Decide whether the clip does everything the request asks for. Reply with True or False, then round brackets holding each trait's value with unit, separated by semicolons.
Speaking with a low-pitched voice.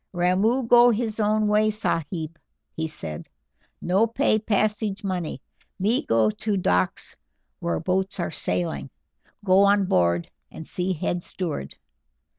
False (185 Hz)